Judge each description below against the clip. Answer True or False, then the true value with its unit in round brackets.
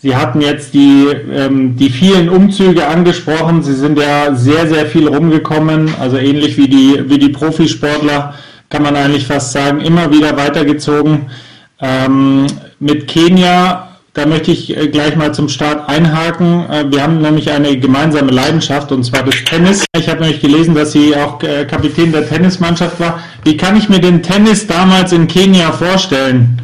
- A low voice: False (150 Hz)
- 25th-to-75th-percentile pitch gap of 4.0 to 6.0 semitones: False (2.6 semitones)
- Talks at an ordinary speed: True (160 wpm)